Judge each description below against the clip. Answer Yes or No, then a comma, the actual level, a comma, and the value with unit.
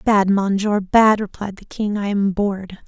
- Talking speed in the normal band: Yes, average, 190 wpm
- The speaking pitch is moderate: No, high, 200 Hz